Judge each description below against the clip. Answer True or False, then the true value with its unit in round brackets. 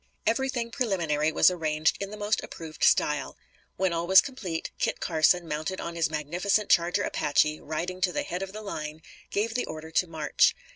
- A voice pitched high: False (175 Hz)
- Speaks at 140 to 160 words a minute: False (185 wpm)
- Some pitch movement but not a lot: True (4.3 semitones)